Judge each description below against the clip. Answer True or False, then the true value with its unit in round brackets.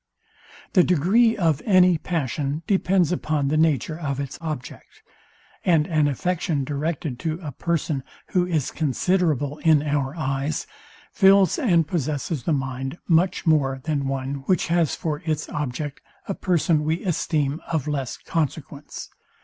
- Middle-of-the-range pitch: True (155 Hz)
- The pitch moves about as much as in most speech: True (3.4 semitones)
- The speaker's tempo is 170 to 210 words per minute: False (140 wpm)